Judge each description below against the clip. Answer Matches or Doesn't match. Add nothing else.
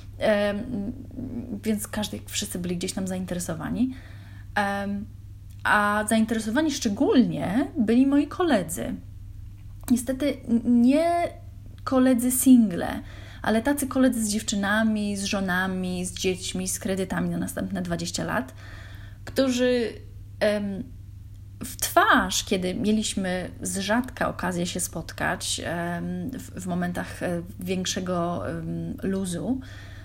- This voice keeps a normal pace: Doesn't match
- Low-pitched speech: Doesn't match